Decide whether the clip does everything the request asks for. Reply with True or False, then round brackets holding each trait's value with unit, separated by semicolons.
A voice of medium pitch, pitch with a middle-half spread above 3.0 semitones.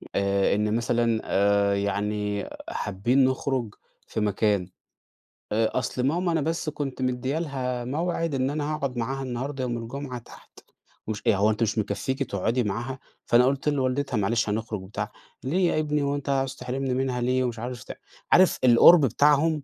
False (125 Hz; 4.2 semitones)